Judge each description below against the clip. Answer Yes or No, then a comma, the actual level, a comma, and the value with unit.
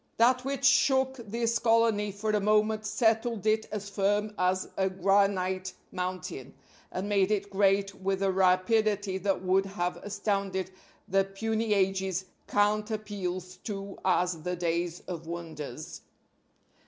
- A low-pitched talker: No, high, 195 Hz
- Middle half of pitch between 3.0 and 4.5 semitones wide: No, narrow, 2.5 semitones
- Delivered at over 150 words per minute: No, slow, 135 wpm